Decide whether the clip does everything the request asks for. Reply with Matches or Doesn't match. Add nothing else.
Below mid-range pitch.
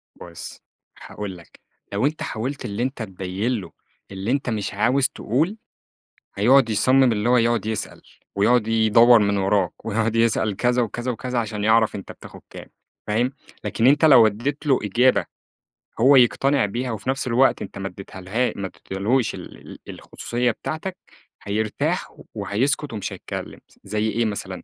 Matches